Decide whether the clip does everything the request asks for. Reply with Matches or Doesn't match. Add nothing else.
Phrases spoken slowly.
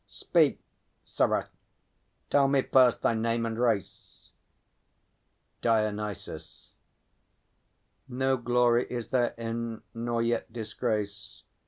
Matches